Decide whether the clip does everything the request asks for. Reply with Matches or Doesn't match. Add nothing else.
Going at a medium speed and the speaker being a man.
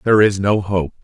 Doesn't match